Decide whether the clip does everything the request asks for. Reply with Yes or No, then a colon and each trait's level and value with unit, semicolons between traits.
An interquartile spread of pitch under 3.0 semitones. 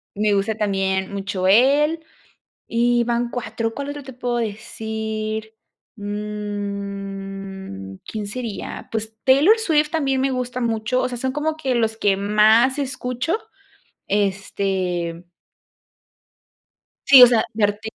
No: average, 4.0 semitones